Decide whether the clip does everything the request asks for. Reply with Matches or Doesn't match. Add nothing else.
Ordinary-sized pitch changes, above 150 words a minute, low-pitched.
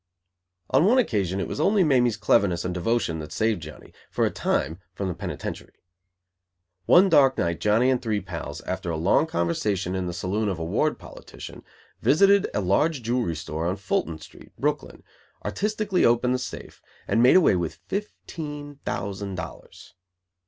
Doesn't match